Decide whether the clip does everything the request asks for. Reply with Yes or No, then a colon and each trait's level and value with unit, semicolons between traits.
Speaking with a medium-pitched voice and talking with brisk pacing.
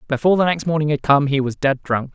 Yes: medium, 145 Hz; fast, 280 wpm